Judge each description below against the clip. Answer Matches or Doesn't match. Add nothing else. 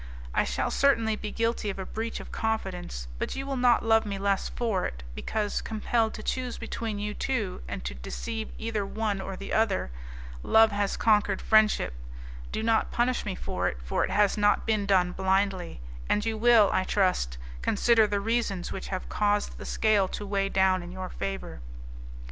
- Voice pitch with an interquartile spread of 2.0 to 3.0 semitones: Matches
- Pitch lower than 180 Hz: Doesn't match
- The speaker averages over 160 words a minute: Matches